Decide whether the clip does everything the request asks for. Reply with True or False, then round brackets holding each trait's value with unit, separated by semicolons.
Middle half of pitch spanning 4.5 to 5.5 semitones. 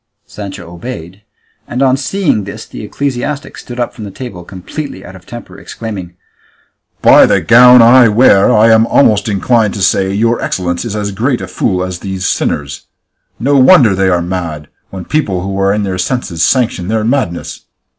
True (4.8 semitones)